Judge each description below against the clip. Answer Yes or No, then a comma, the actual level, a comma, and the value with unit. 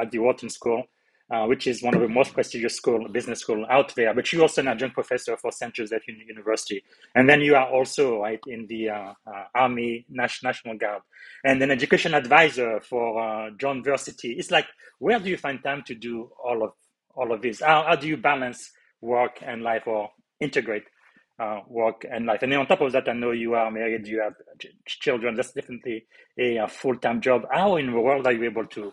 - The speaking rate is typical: No, fast, 215 wpm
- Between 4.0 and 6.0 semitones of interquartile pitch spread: No, average, 3.6 semitones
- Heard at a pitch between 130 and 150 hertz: No, low, 120 Hz